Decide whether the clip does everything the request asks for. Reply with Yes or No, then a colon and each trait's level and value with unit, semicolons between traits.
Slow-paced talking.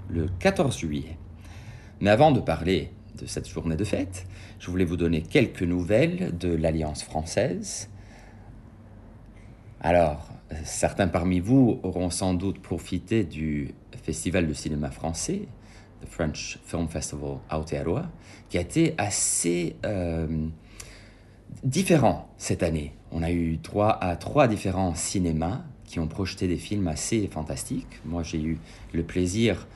Yes: slow, 135 wpm